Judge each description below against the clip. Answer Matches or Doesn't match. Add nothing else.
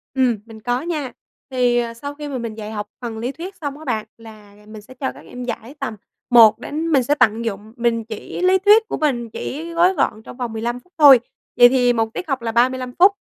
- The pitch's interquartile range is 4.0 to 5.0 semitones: Matches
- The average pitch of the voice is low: Doesn't match